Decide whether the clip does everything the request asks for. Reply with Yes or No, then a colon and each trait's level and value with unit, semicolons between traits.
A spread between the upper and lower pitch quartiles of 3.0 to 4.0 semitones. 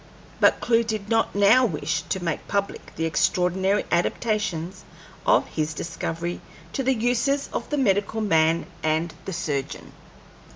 No: wide, 5.5 semitones